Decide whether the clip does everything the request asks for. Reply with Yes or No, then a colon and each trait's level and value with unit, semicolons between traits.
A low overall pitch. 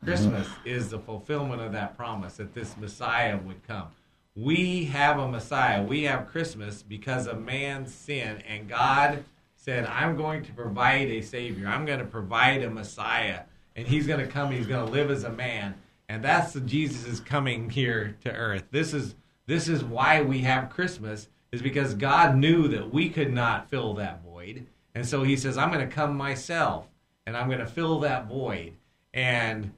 Yes: low, 125 Hz